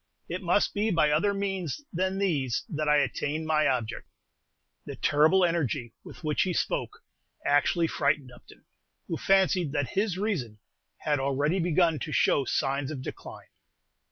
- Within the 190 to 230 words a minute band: No, average, 155 wpm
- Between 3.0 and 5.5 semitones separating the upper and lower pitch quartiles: Yes, average, 4.5 semitones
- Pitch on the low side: No, medium, 155 Hz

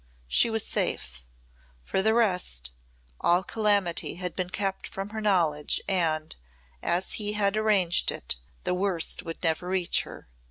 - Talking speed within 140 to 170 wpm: Yes, average, 150 wpm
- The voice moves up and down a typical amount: Yes, average, 3.7 semitones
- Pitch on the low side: No, medium, 185 Hz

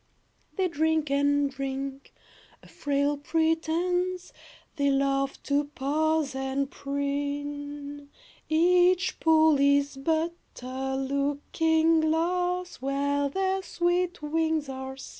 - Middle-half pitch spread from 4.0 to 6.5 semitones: No, narrow, 2.6 semitones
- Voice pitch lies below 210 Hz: No, very high, 290 Hz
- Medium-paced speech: No, slow, 105 wpm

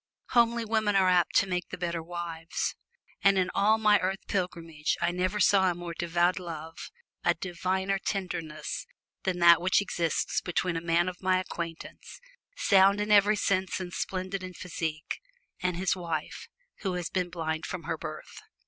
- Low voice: No, medium, 180 Hz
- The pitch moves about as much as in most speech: No, narrow, 2.1 semitones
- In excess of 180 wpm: No, average, 170 wpm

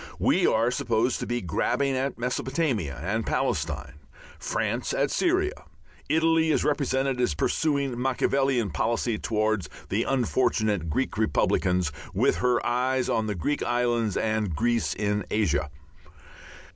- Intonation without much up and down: No, average, 3.8 semitones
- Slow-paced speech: Yes, slow, 130 wpm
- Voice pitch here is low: Yes, low, 120 Hz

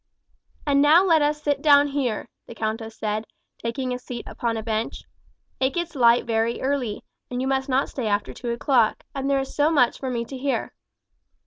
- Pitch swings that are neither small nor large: Yes, average, 3.4 semitones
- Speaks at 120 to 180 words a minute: No, average, 200 wpm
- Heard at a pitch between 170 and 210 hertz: No, very high, 260 Hz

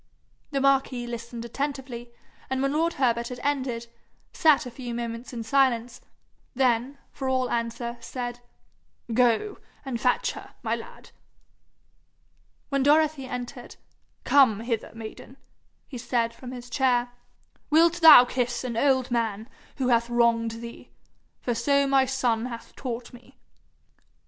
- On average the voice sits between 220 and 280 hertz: Yes, high, 245 Hz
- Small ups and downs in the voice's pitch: Yes, narrow, 2.3 semitones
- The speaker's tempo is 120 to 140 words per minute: Yes, slow, 135 wpm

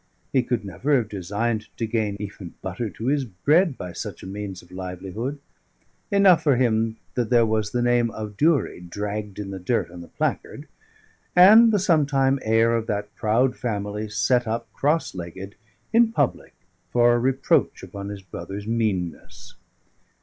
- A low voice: Yes, low, 110 Hz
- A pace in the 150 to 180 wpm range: Yes, average, 165 wpm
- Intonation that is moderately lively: Yes, average, 4.2 semitones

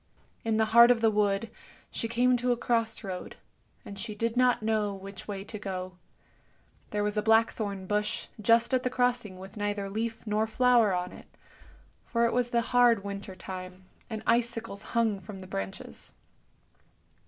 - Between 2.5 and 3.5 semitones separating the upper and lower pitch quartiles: Yes, average, 2.8 semitones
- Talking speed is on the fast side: No, average, 175 wpm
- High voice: Yes, high, 215 Hz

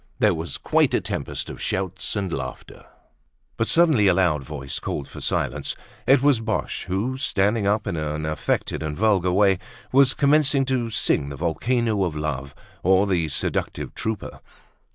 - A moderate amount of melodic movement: No, wide, 6.5 semitones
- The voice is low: Yes, very low, 95 Hz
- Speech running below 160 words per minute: No, average, 165 wpm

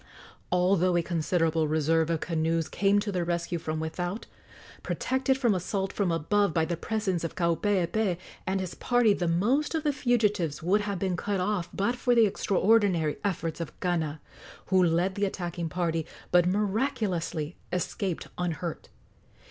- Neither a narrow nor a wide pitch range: Yes, average, 3.5 semitones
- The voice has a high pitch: No, medium, 180 Hz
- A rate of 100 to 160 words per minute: Yes, average, 155 wpm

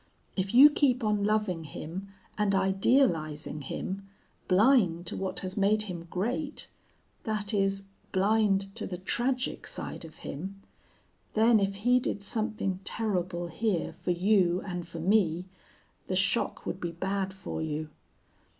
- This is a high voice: Yes, high, 195 Hz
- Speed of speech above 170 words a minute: No, average, 140 wpm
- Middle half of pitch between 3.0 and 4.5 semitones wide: Yes, average, 3.4 semitones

